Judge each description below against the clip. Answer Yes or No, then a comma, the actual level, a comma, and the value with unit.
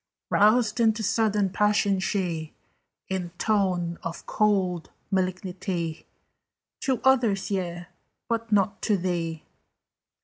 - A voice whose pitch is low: No, high, 195 Hz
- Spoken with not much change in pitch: No, average, 3.2 semitones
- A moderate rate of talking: No, slow, 100 wpm